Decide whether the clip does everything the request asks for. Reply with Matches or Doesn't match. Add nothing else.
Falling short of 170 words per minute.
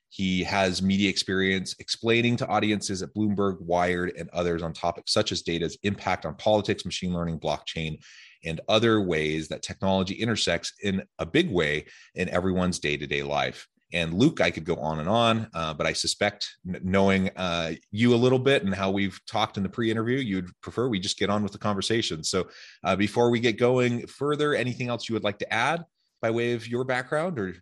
Doesn't match